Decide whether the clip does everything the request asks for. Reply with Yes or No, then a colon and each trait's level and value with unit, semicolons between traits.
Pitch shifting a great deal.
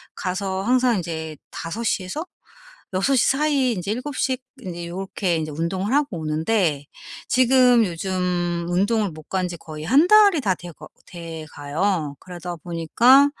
Yes: wide, 6.4 semitones